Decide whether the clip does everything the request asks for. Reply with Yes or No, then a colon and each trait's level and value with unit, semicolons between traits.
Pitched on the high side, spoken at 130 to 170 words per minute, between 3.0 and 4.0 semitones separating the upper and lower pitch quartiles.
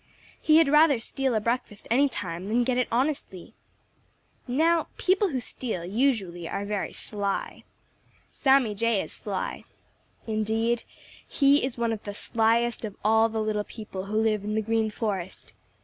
Yes: high, 225 Hz; average, 160 wpm; average, 3.6 semitones